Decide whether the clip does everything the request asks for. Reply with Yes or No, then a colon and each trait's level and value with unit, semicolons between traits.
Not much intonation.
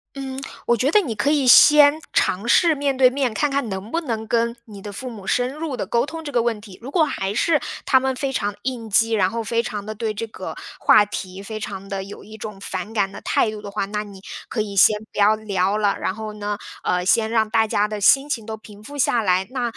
No: average, 4.0 semitones